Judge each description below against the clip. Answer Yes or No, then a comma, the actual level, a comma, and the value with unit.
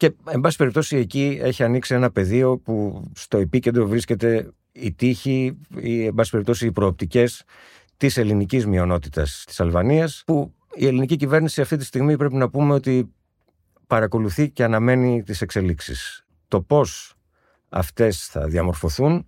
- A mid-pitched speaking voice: No, low, 125 Hz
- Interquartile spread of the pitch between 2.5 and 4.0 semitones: No, average, 4.7 semitones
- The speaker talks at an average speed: Yes, average, 145 wpm